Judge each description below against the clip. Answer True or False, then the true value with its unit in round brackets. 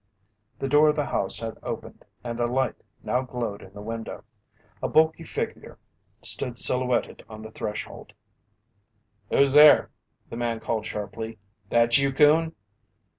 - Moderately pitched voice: False (120 Hz)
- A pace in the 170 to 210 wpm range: False (145 wpm)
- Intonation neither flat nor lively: True (3.6 semitones)